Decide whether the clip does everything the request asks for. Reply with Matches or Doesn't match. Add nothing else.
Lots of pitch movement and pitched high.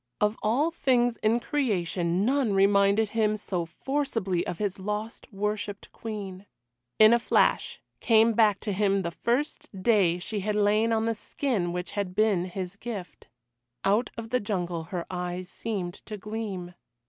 Doesn't match